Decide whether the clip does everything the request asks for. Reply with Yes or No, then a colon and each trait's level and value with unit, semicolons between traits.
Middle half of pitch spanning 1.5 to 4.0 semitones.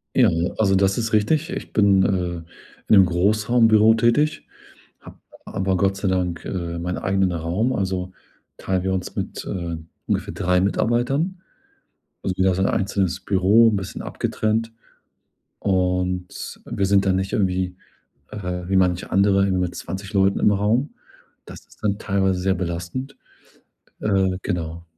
Yes: narrow, 2.5 semitones